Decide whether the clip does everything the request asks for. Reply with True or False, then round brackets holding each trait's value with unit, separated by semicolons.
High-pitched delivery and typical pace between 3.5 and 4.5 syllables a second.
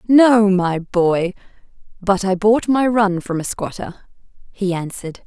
True (195 Hz; 4.0 syllables/s)